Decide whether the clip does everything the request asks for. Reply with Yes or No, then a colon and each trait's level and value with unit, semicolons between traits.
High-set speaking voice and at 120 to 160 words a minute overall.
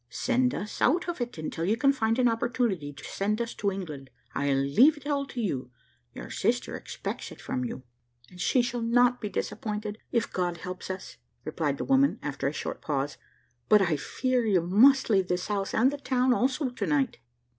No: high, 215 Hz; average, 200 wpm